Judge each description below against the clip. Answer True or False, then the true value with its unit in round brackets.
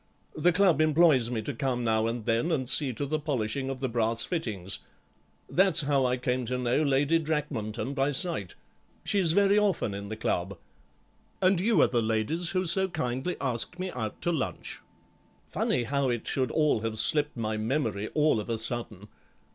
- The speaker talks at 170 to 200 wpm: True (185 wpm)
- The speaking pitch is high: False (130 Hz)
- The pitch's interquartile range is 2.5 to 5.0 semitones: False (5.6 semitones)